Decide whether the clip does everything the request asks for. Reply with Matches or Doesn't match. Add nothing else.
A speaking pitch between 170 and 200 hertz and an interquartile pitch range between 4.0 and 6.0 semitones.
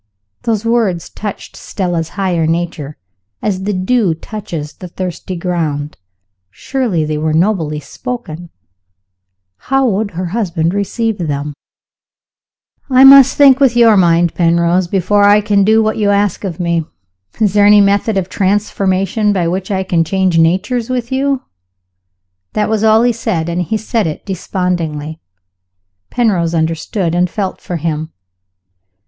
Matches